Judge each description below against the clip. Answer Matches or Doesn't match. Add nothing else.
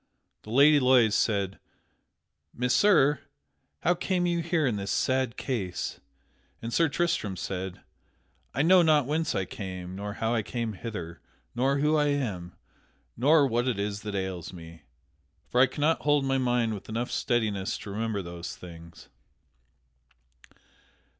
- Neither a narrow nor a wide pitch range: Doesn't match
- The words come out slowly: Doesn't match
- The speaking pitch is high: Doesn't match